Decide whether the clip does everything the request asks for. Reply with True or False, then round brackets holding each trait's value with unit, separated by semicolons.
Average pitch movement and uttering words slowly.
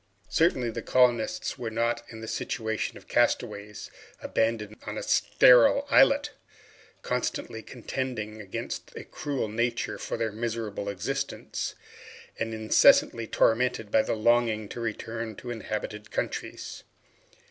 False (1.9 semitones; 125 wpm)